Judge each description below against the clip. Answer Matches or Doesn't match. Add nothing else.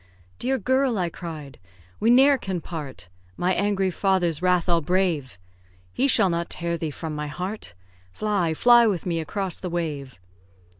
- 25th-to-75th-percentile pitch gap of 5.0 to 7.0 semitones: Doesn't match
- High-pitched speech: Doesn't match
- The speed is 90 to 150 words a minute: Doesn't match